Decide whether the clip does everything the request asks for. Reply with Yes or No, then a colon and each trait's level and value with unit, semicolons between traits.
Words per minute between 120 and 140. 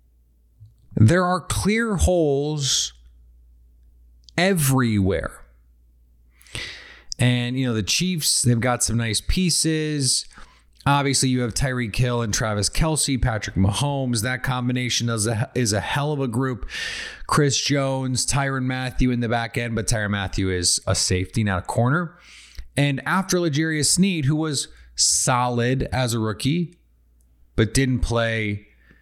Yes: slow, 135 wpm